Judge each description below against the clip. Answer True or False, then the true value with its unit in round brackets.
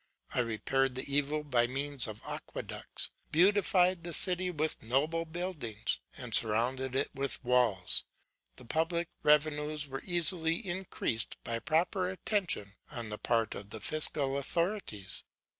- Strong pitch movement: True (6.0 semitones)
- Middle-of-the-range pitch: True (145 Hz)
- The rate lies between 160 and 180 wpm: False (135 wpm)